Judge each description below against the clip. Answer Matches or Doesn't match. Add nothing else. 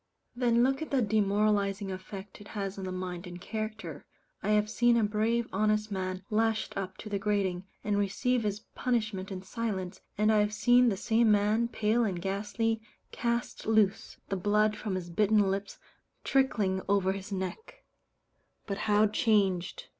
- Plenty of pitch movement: Doesn't match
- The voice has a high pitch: Matches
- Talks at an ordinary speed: Matches